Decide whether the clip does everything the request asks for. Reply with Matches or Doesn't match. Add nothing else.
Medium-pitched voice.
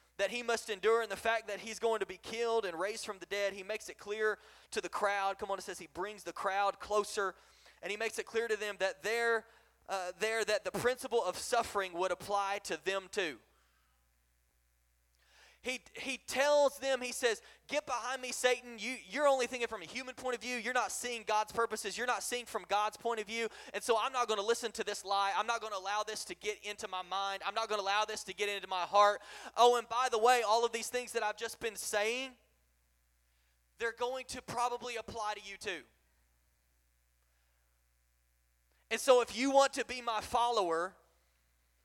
Doesn't match